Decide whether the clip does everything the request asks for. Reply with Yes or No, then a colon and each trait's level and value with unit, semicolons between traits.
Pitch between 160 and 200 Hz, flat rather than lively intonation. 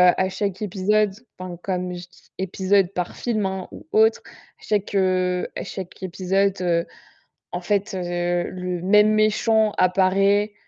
Yes: high, 190 Hz; narrow, 2.2 semitones